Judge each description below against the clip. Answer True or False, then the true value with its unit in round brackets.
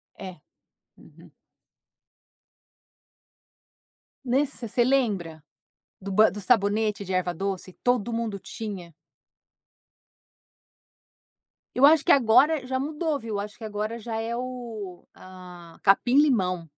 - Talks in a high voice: True (220 Hz)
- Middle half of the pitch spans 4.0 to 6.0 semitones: True (4.7 semitones)